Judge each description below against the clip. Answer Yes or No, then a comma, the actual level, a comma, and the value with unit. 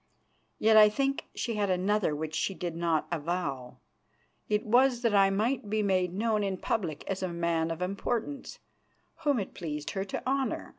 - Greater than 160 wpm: Yes, average, 180 wpm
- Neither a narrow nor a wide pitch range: Yes, average, 4.4 semitones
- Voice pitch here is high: Yes, high, 195 Hz